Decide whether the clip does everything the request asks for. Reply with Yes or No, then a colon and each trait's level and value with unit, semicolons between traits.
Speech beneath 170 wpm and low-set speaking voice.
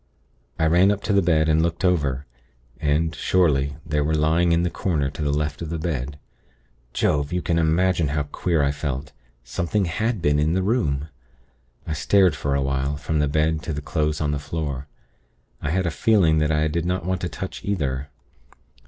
No: average, 200 wpm; very low, 80 Hz